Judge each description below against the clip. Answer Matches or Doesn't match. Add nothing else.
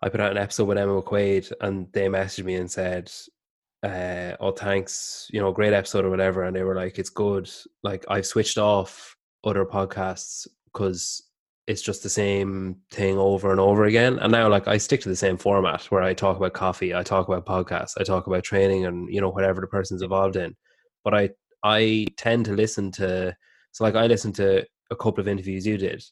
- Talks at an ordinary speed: Doesn't match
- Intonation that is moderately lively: Doesn't match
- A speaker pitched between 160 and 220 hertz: Doesn't match